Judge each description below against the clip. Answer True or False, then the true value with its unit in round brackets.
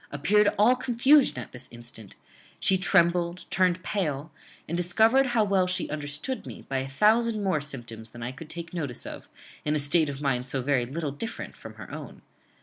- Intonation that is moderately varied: False (6.7 semitones)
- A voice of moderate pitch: True (165 Hz)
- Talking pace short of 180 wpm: False (190 wpm)